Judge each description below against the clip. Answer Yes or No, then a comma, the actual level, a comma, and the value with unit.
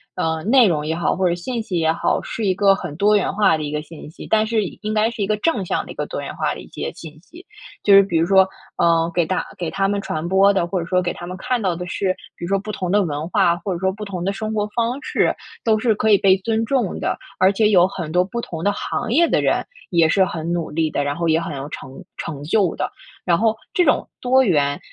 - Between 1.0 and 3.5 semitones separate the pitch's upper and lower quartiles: No, average, 4.1 semitones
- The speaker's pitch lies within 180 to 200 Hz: Yes, high, 190 Hz